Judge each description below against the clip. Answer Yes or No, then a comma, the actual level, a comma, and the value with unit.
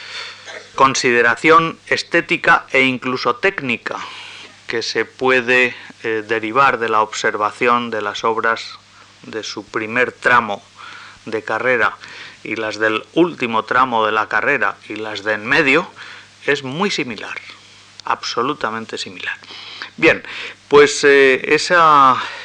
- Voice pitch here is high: No, low, 120 Hz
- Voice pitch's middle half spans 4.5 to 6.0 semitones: No, average, 4.0 semitones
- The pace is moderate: No, slow, 120 wpm